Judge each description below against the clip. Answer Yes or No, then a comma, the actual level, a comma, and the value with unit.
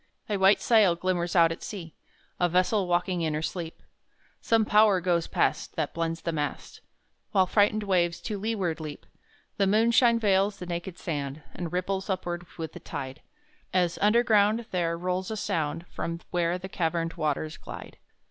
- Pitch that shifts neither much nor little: Yes, average, 3.2 semitones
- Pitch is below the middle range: No, medium, 180 Hz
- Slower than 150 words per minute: No, average, 165 wpm